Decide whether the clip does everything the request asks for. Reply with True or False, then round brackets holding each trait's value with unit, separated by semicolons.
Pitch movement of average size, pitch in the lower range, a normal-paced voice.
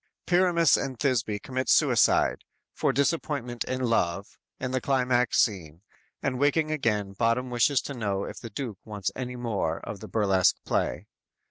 True (4.4 semitones; 120 Hz; 160 wpm)